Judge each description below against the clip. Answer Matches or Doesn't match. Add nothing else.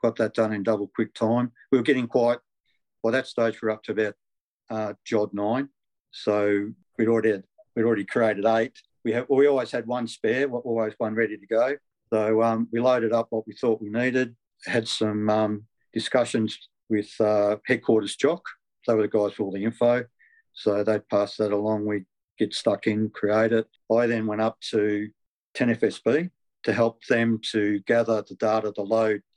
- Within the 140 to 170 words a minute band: Doesn't match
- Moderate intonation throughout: Doesn't match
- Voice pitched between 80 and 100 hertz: Doesn't match